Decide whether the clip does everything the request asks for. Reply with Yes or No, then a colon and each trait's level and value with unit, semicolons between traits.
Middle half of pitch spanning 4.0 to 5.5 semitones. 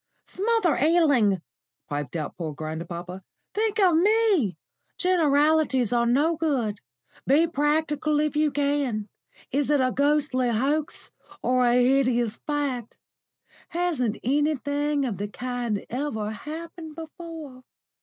Yes: average, 4.7 semitones